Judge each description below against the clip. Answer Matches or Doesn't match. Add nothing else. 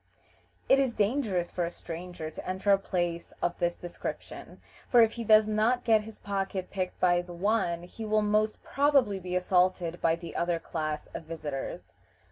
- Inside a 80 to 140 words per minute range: Doesn't match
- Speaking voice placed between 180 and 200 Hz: Matches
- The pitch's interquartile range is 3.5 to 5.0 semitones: Matches